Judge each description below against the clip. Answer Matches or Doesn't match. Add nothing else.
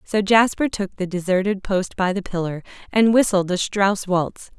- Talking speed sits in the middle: Matches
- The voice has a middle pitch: Doesn't match